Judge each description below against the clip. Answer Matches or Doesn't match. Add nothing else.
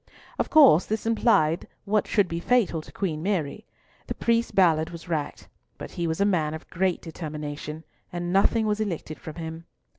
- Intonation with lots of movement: Doesn't match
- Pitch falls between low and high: Matches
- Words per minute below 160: Doesn't match